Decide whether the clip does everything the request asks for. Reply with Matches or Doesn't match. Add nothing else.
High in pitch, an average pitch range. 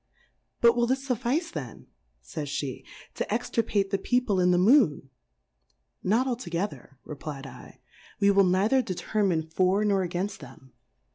Doesn't match